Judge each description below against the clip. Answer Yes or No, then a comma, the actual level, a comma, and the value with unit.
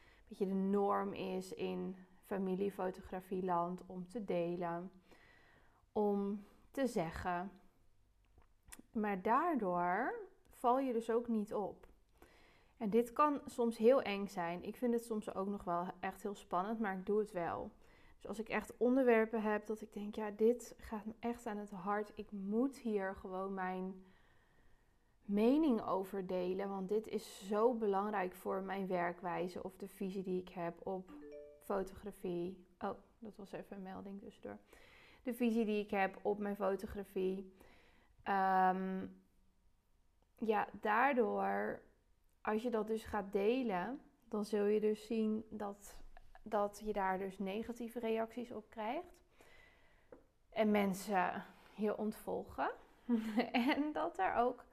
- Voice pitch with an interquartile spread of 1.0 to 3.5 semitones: Yes, average, 3.2 semitones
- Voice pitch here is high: Yes, high, 205 Hz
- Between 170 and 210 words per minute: No, average, 145 wpm